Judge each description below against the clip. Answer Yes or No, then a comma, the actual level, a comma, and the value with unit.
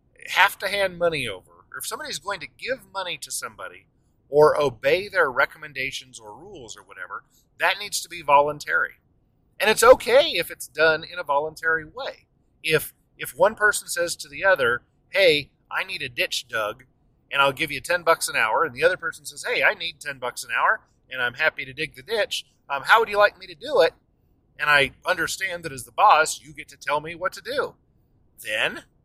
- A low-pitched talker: No, medium, 160 Hz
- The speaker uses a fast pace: Yes, fast, 215 wpm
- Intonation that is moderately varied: No, wide, 6.2 semitones